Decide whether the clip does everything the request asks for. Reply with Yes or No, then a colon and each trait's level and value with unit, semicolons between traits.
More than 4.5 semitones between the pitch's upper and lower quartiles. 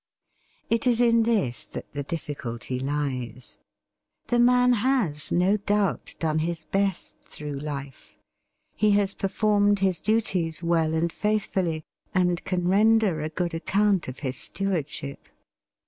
Yes: wide, 5.5 semitones